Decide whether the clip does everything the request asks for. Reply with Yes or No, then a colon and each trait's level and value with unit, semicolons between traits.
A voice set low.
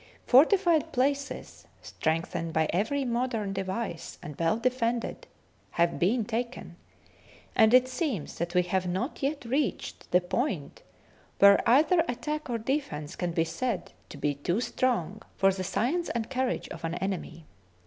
No: high, 230 Hz